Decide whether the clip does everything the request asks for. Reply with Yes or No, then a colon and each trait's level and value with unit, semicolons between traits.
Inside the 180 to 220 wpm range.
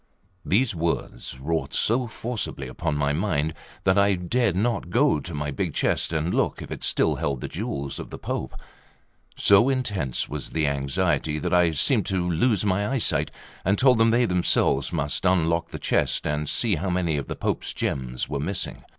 Yes: average, 185 wpm